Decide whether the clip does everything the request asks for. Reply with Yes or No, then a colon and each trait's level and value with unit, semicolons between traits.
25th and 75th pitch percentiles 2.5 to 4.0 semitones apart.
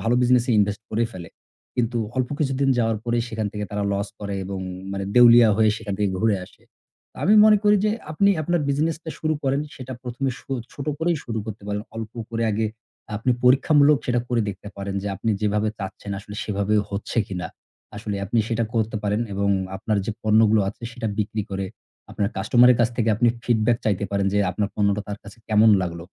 Yes: average, 3.1 semitones